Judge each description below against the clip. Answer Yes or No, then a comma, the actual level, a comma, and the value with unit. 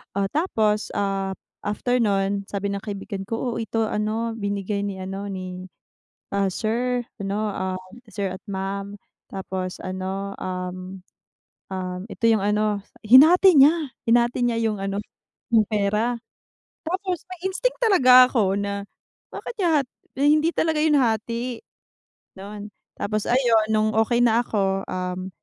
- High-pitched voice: Yes, high, 210 Hz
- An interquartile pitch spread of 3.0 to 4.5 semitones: Yes, average, 3.7 semitones